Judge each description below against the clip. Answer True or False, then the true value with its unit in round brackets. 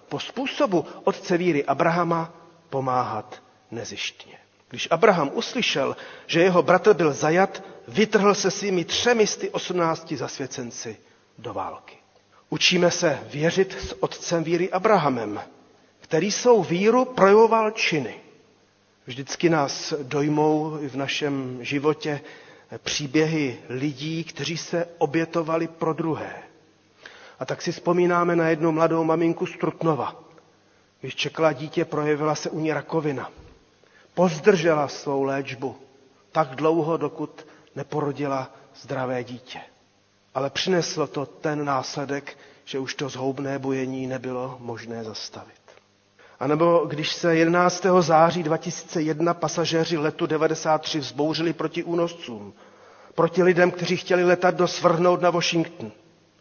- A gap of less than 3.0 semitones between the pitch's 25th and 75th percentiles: False (3.7 semitones)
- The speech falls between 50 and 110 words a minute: False (120 wpm)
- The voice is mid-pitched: True (160 Hz)